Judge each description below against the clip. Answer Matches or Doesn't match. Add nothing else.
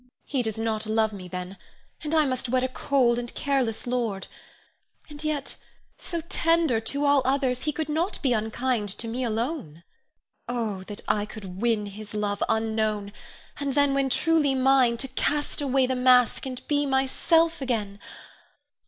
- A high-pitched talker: Matches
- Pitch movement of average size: Matches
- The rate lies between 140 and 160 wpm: Doesn't match